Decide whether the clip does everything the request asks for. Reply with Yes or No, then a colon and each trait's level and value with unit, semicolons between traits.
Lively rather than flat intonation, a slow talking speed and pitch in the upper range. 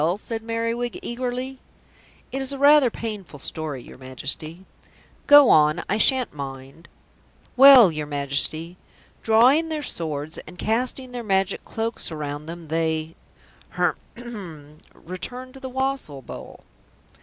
Yes: wide, 8.4 semitones; slow, 125 wpm; high, 200 Hz